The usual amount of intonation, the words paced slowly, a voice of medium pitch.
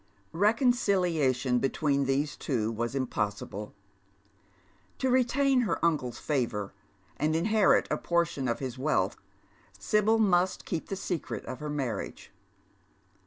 No: wide, 7.5 semitones; slow, 120 wpm; medium, 150 Hz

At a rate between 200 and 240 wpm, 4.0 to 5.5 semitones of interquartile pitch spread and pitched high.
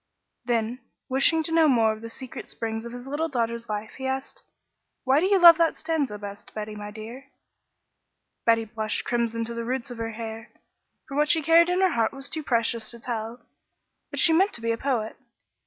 Yes: fast, 205 wpm; average, 4.4 semitones; high, 235 Hz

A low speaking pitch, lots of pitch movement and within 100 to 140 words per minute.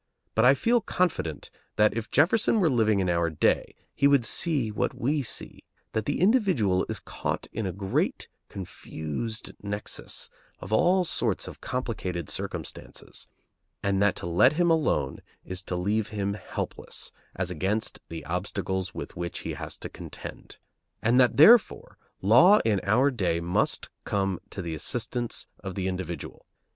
No: low, 105 Hz; wide, 6.1 semitones; average, 155 wpm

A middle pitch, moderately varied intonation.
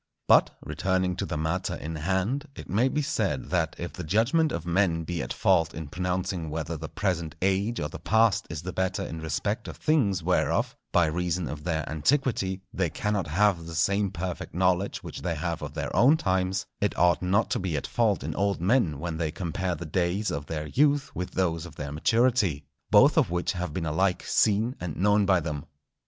No: very low, 90 Hz; average, 3.7 semitones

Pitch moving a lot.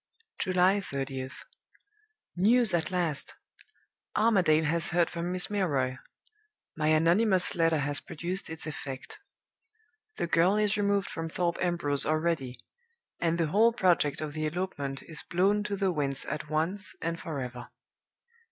No: average, 3.6 semitones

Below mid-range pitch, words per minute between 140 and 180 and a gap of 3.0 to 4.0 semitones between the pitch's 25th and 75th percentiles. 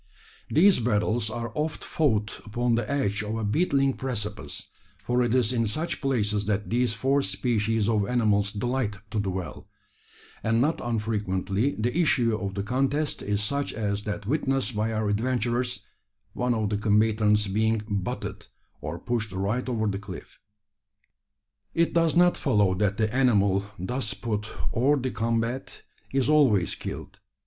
Yes: low, 110 Hz; average, 155 wpm; average, 3.5 semitones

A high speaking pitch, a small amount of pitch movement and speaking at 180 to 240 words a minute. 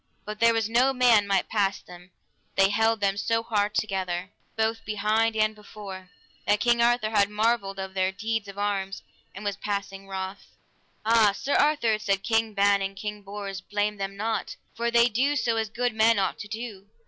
Yes: high, 210 Hz; narrow, 2.3 semitones; average, 185 wpm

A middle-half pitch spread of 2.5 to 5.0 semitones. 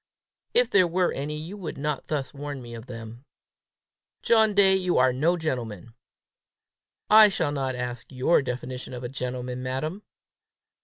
No: wide, 5.6 semitones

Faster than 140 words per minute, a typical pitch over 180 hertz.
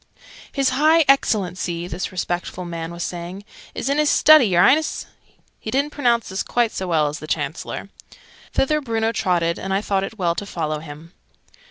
Yes: average, 175 wpm; high, 190 Hz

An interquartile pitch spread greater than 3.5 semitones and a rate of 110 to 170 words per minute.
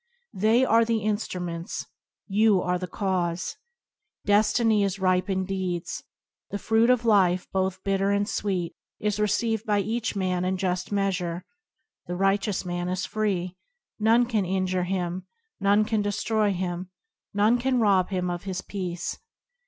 No: average, 2.7 semitones; average, 150 wpm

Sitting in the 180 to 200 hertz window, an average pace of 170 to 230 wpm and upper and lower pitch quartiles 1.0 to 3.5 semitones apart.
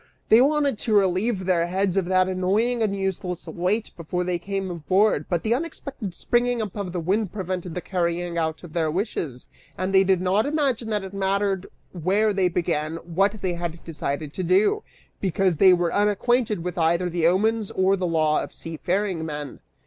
Yes: medium, 185 Hz; average, 185 wpm; average, 3.2 semitones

